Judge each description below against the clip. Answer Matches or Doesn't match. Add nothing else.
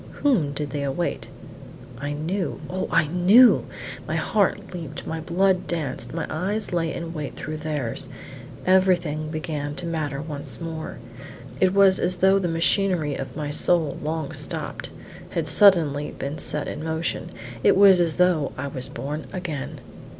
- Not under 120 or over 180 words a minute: Matches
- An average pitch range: Matches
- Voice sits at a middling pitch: Matches